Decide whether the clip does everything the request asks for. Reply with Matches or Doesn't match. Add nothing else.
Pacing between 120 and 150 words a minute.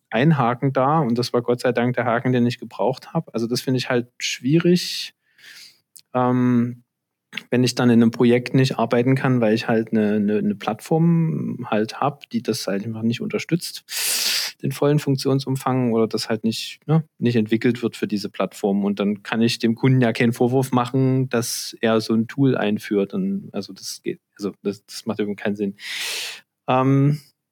Doesn't match